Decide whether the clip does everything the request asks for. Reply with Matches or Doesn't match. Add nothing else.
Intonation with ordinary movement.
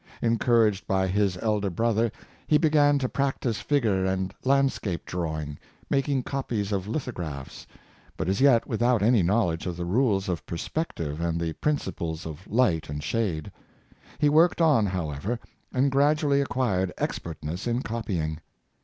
Doesn't match